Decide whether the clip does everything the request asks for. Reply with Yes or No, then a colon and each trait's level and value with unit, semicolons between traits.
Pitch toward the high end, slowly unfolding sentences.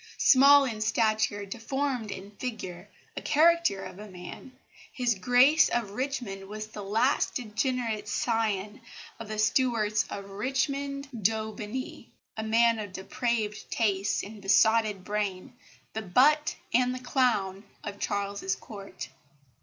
Yes: high, 220 Hz; slow, 130 wpm